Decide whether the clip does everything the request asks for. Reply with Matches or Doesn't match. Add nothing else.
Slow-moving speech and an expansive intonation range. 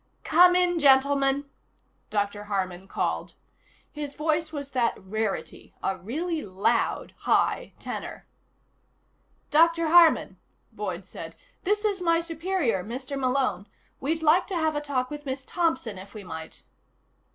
Matches